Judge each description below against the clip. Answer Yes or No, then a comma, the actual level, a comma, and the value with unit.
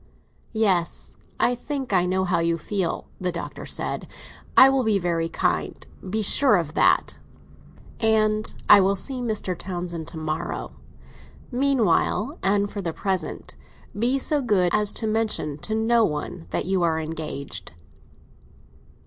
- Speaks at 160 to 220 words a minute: No, average, 140 wpm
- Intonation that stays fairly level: No, average, 4.7 semitones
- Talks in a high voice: Yes, high, 195 Hz